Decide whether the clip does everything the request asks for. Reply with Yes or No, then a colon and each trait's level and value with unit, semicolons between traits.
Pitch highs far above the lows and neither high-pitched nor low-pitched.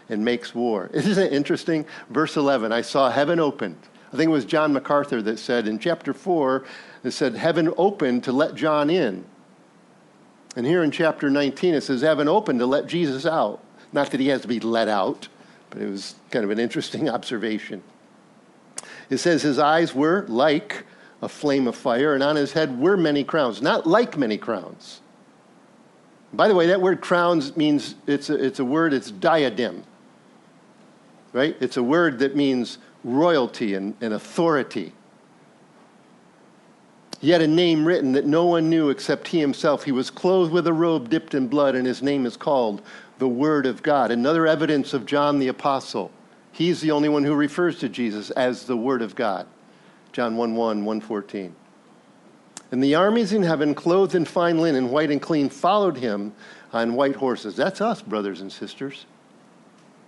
No: average, 4.6 semitones; medium, 145 Hz